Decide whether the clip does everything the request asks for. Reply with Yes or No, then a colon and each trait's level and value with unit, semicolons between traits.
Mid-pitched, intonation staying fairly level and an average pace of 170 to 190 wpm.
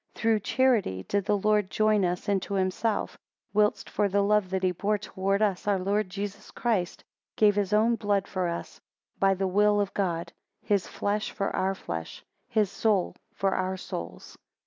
No: high, 200 Hz; narrow, 2.0 semitones; average, 180 wpm